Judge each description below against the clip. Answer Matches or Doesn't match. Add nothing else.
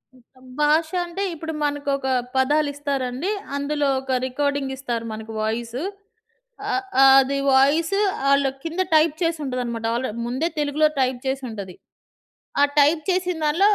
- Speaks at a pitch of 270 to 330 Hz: Matches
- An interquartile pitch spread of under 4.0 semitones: Matches